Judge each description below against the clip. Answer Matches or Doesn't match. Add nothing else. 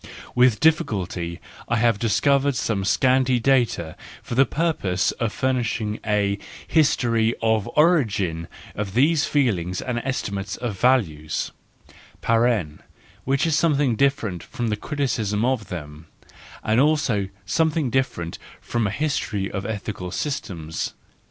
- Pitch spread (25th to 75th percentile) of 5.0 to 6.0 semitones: Matches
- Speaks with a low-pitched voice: Matches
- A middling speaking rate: Doesn't match